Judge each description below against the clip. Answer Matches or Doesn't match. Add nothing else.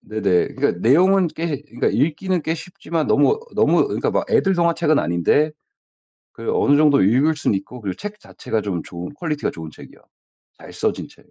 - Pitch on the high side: Doesn't match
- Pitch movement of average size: Doesn't match